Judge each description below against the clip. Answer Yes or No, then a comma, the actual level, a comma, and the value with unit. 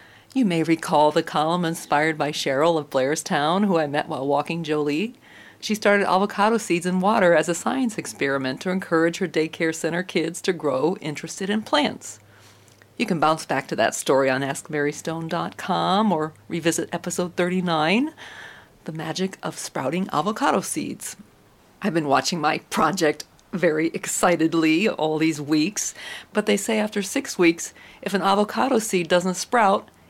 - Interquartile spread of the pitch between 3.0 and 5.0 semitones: Yes, average, 4.0 semitones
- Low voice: No, medium, 170 Hz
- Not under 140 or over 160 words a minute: Yes, average, 155 wpm